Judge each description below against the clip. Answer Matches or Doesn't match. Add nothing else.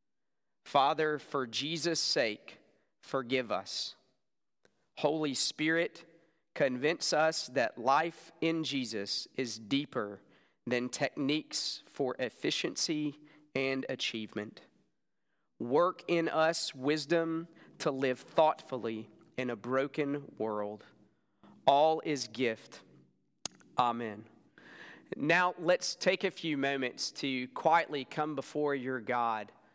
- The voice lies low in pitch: Doesn't match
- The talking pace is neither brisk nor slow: Doesn't match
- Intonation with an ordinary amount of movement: Matches